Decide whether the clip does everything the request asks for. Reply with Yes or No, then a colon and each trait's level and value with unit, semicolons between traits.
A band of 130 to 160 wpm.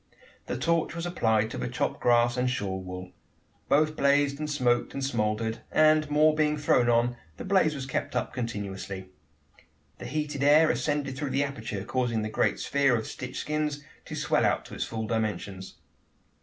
No: average, 180 wpm